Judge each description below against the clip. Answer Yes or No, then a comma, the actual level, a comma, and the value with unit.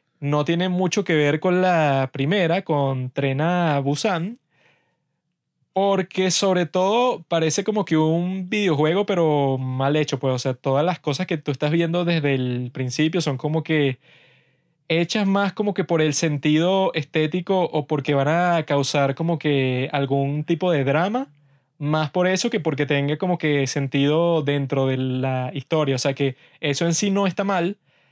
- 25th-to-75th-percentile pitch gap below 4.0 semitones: No, average, 4.3 semitones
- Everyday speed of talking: Yes, average, 170 wpm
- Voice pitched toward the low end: No, medium, 155 Hz